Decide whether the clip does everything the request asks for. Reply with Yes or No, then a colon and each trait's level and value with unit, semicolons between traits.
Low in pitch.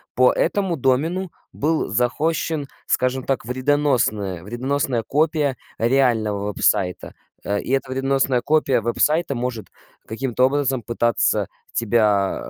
Yes: low, 130 Hz